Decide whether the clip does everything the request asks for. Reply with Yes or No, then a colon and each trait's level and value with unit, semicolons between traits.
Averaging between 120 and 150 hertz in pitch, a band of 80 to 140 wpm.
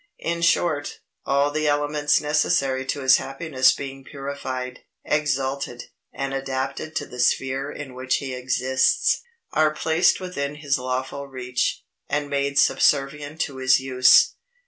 Yes: medium, 140 Hz; slow, 135 wpm